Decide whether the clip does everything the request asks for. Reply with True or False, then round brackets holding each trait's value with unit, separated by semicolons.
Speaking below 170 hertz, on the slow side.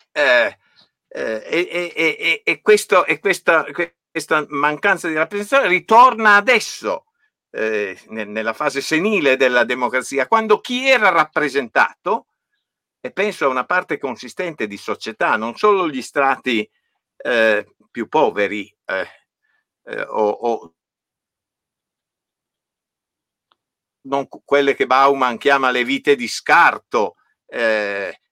True (140 Hz; 110 wpm)